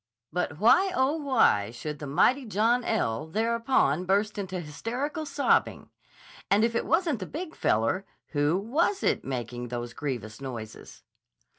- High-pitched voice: Yes, high, 195 Hz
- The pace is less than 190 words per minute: Yes, average, 145 wpm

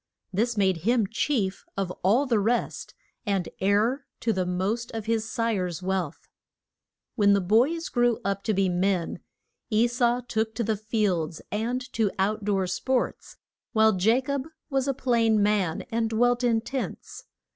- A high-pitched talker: Yes, high, 220 Hz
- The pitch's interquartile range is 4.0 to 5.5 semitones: No, average, 3.6 semitones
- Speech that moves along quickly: No, average, 160 wpm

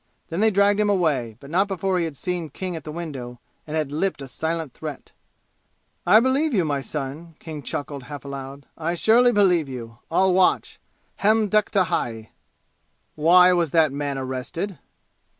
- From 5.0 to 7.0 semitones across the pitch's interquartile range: Yes, wide, 5.4 semitones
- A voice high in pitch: No, medium, 165 Hz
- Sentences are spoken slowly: No, average, 170 wpm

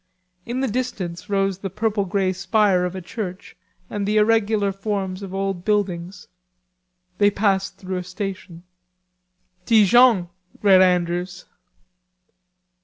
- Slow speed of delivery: Yes, slow, 120 wpm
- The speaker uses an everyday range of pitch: No, narrow, 2.2 semitones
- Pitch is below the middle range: No, high, 195 Hz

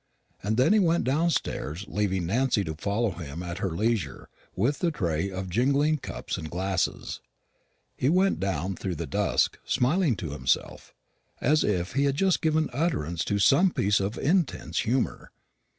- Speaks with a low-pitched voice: Yes, low, 105 Hz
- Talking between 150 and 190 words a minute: Yes, average, 165 wpm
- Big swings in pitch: Yes, wide, 8.2 semitones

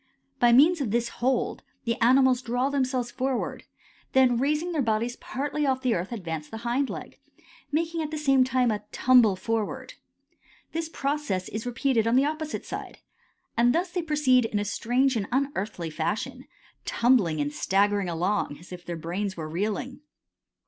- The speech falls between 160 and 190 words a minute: Yes, average, 170 wpm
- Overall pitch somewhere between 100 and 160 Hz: No, high, 245 Hz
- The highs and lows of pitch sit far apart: No, average, 4.9 semitones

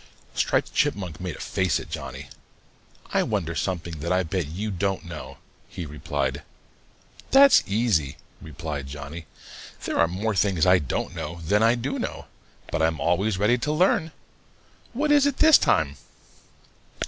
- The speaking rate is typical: Yes, average, 155 wpm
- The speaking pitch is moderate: No, very low, 90 Hz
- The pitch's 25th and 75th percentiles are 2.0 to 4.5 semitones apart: No, wide, 5.4 semitones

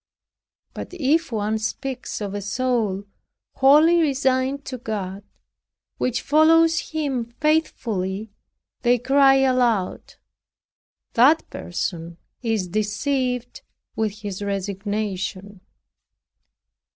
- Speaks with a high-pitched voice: Yes, high, 235 Hz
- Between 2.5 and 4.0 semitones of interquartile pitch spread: No, average, 5.0 semitones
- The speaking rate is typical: No, slow, 90 wpm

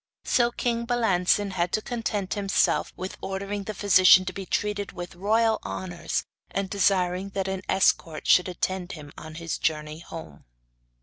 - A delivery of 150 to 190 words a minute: Yes, average, 160 wpm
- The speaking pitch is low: No, high, 190 Hz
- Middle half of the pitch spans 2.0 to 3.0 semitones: Yes, narrow, 2.5 semitones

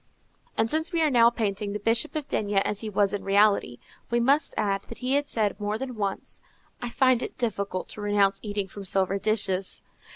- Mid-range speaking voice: No, high, 210 Hz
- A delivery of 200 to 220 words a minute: Yes, fast, 205 wpm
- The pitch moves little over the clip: No, average, 3.2 semitones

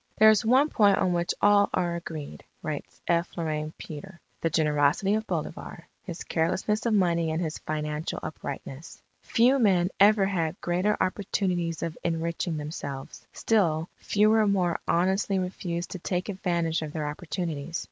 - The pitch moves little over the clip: No, average, 3.7 semitones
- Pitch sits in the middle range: Yes, medium, 175 Hz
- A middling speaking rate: Yes, average, 155 wpm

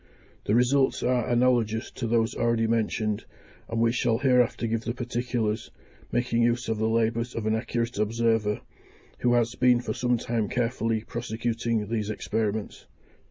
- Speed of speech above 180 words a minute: No, average, 155 wpm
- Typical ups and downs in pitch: No, narrow, 1.5 semitones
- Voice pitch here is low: Yes, low, 115 Hz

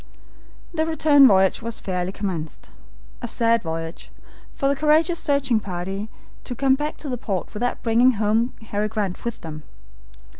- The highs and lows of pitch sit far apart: Yes, wide, 6.0 semitones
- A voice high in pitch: Yes, high, 230 Hz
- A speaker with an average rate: Yes, average, 155 wpm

